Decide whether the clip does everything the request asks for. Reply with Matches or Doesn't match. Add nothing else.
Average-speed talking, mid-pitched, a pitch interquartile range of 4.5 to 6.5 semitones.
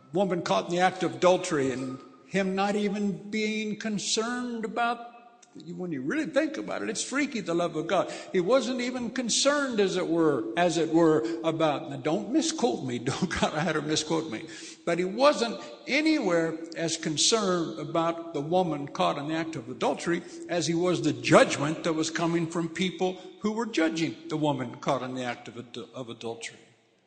Matches